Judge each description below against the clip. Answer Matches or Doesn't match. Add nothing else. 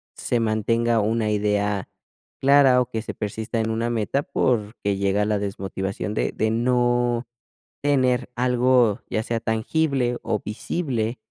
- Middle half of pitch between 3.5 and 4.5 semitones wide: Doesn't match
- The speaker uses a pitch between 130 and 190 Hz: Doesn't match